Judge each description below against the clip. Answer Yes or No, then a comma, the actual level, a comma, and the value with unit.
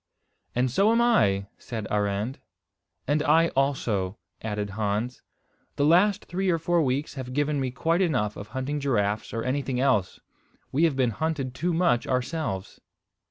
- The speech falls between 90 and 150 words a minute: No, average, 160 wpm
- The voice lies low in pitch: Yes, low, 130 Hz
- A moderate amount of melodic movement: No, wide, 6.4 semitones